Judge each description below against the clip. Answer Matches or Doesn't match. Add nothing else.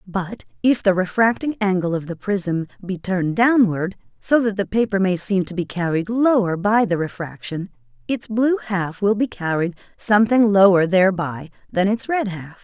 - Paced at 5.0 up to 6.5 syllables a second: Doesn't match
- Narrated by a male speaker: Doesn't match